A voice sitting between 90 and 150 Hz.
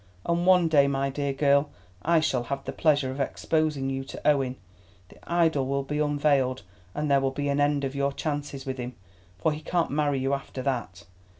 Yes: medium, 140 Hz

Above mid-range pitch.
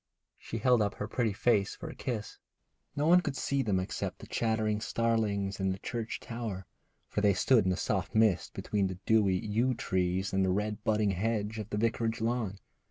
No: low, 105 Hz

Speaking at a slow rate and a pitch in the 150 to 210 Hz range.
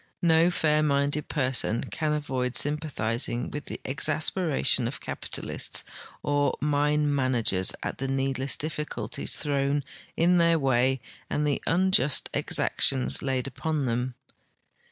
No: slow, 125 wpm; medium, 140 Hz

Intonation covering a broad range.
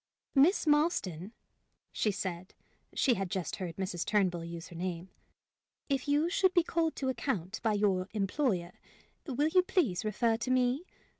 Yes: wide, 7.7 semitones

